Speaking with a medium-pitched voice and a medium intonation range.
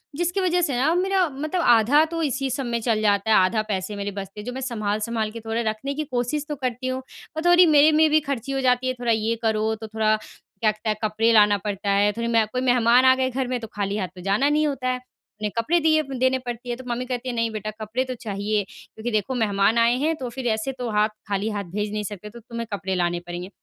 No: high, 235 Hz; average, 3.7 semitones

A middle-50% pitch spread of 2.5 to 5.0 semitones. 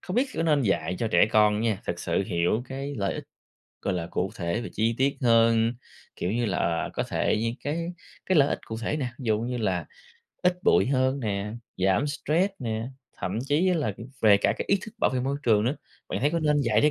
No: wide, 5.5 semitones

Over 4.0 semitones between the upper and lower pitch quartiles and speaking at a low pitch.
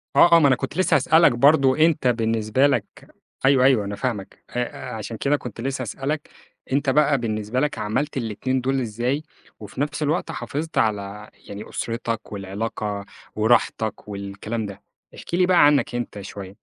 Yes: average, 4.8 semitones; low, 120 Hz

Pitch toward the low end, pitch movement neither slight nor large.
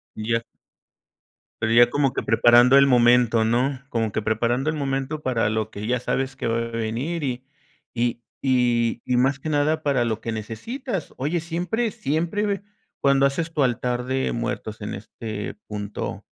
Yes: low, 125 Hz; average, 3.7 semitones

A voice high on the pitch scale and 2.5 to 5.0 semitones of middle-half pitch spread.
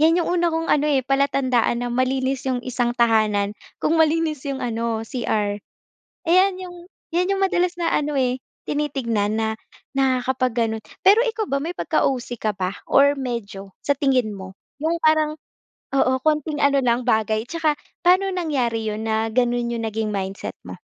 No: very high, 260 Hz; wide, 5.4 semitones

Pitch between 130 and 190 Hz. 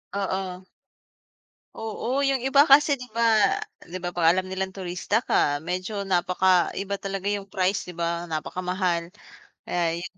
Yes: medium, 185 Hz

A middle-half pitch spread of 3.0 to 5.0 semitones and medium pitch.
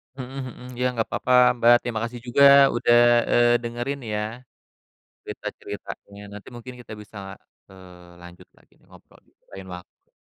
No: average, 4.2 semitones; low, 120 Hz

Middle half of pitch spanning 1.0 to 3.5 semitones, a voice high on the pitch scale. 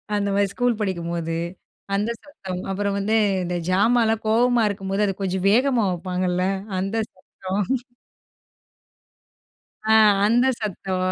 Yes: average, 3.2 semitones; high, 200 Hz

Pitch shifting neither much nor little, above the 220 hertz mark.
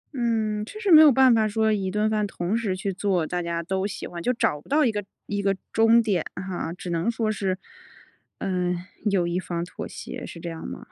No: average, 3.8 semitones; high, 200 Hz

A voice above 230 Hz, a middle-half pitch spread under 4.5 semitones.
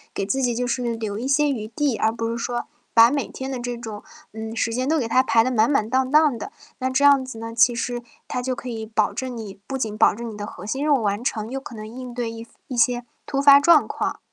Yes: high, 240 Hz; average, 2.8 semitones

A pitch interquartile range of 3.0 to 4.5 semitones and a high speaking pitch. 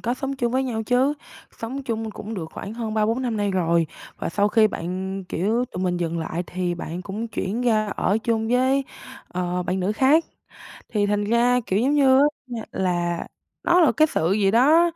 No: average, 5.1 semitones; high, 215 Hz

